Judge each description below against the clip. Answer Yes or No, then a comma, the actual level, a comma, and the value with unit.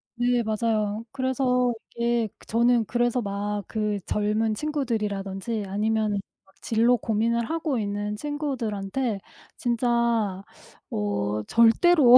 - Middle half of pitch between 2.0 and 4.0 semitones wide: Yes, average, 2.7 semitones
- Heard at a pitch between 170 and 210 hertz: No, high, 225 Hz